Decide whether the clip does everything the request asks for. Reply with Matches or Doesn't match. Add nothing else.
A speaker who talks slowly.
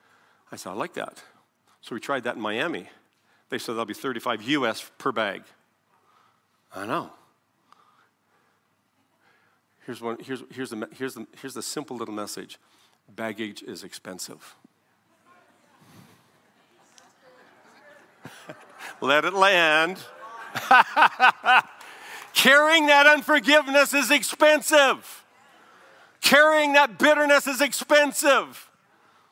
Matches